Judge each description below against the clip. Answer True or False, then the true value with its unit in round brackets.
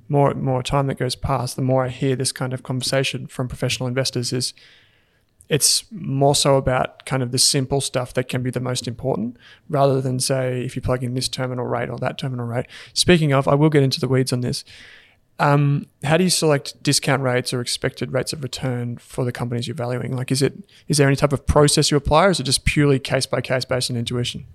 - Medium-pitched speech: False (130 Hz)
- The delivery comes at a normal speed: False (235 wpm)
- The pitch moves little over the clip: True (1.8 semitones)